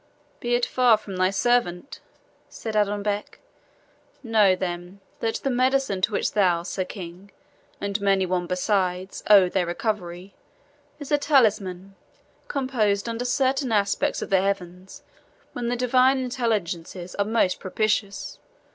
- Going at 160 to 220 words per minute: No, slow, 135 wpm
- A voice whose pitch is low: No, high, 200 Hz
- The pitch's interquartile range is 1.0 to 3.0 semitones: No, average, 4.5 semitones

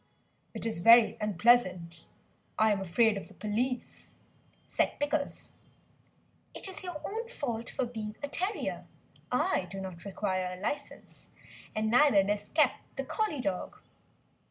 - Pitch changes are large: Yes, wide, 6.4 semitones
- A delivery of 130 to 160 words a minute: Yes, average, 140 wpm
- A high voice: Yes, high, 225 Hz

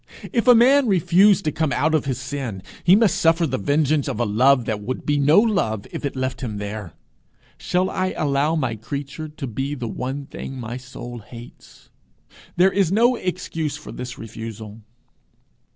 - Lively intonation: Yes, wide, 5.7 semitones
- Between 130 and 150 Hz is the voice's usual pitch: Yes, medium, 140 Hz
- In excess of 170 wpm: Yes, average, 180 wpm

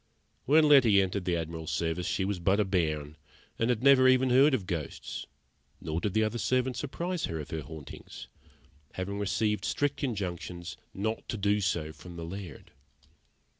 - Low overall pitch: Yes, low, 100 Hz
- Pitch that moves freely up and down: Yes, wide, 6.4 semitones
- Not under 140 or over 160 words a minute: No, average, 170 wpm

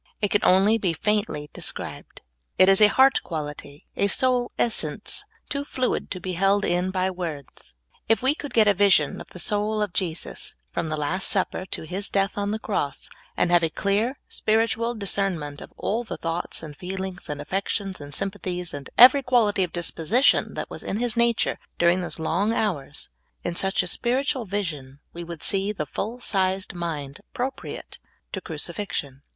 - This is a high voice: Yes, high, 195 Hz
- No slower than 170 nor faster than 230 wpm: Yes, average, 180 wpm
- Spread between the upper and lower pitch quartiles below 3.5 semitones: No, average, 4.1 semitones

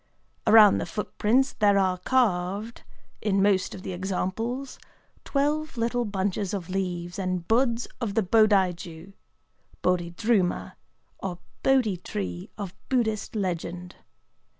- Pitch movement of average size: Yes, average, 4.0 semitones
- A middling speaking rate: No, slow, 120 wpm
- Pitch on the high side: Yes, high, 200 Hz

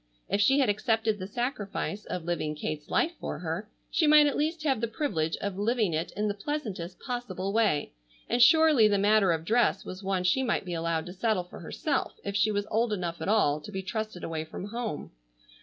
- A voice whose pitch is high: Yes, high, 205 Hz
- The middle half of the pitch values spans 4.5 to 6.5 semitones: Yes, average, 4.9 semitones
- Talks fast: Yes, fast, 215 wpm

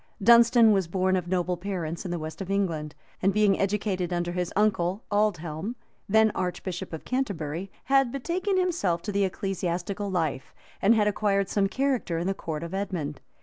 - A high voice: Yes, high, 195 Hz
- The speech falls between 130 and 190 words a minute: Yes, average, 175 wpm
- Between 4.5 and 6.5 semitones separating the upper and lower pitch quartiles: No, average, 3.3 semitones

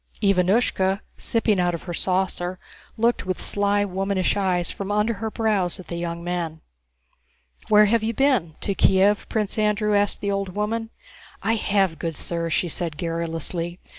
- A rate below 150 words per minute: No, average, 165 wpm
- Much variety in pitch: No, average, 3.2 semitones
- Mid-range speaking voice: No, high, 195 Hz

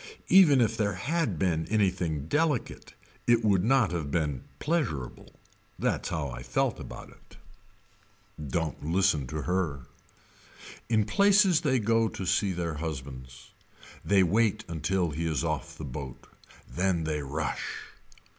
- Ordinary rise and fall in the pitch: No, wide, 6.5 semitones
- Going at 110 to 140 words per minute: Yes, slow, 135 wpm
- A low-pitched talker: Yes, very low, 90 Hz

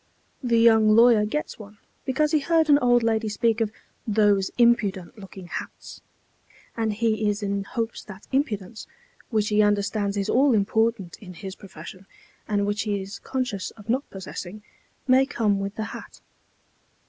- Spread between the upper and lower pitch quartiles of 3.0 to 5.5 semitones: No, narrow, 2.6 semitones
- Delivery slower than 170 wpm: Yes, average, 160 wpm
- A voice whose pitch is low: No, high, 215 Hz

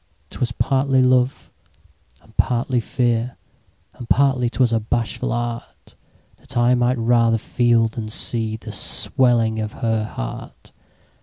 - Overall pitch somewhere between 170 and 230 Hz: No, low, 120 Hz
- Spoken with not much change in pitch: Yes, narrow, 1.8 semitones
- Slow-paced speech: Yes, slow, 110 wpm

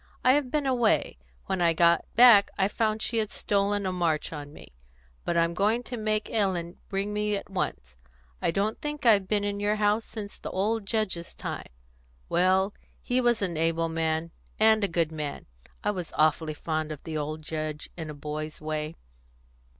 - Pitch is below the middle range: No, high, 190 Hz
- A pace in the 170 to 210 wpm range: Yes, average, 190 wpm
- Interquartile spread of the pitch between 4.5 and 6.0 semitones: Yes, average, 5.0 semitones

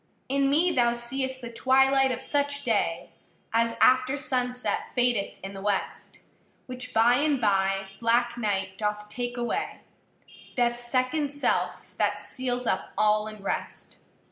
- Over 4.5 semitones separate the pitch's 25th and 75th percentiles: No, average, 3.1 semitones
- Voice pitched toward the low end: No, high, 245 Hz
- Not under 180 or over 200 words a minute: No, average, 140 wpm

